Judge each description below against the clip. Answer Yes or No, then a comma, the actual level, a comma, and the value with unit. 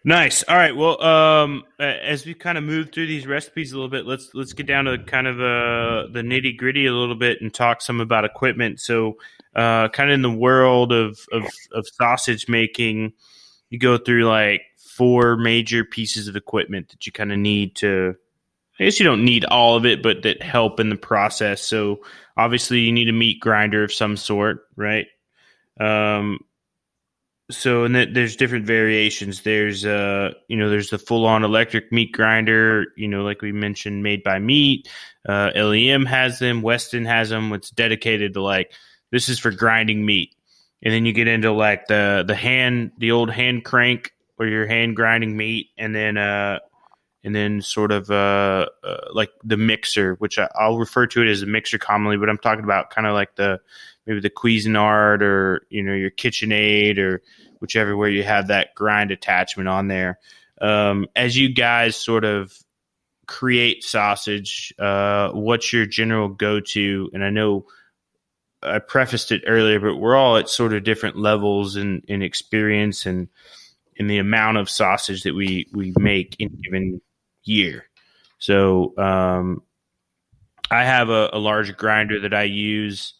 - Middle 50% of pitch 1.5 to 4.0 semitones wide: Yes, narrow, 2.5 semitones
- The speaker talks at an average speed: Yes, average, 180 wpm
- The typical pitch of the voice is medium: No, low, 110 Hz